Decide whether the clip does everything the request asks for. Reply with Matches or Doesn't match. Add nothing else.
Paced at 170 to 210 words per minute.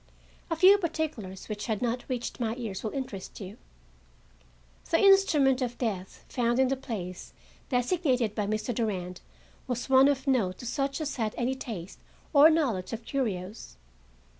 Doesn't match